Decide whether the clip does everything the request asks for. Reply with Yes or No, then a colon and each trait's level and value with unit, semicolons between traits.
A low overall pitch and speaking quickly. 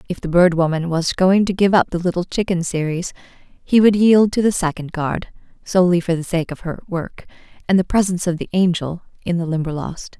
No: medium, 175 Hz; fast, 210 wpm